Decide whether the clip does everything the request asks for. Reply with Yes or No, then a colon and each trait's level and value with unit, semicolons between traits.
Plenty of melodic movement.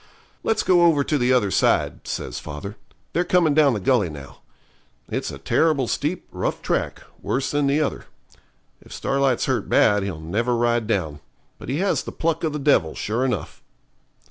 Yes: wide, 6.7 semitones